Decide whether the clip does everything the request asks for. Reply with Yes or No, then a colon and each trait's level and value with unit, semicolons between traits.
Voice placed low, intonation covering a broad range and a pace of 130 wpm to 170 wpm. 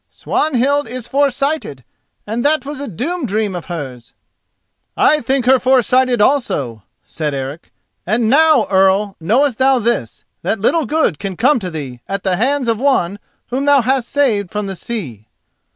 No: high, 235 Hz; wide, 6.3 semitones; average, 165 wpm